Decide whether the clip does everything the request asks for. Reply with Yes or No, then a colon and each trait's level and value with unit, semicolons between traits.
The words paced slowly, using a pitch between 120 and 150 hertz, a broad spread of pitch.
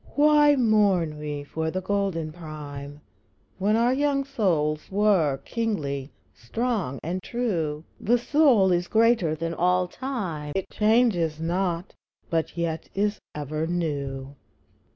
No: slow, 130 wpm; medium, 175 Hz; wide, 6.2 semitones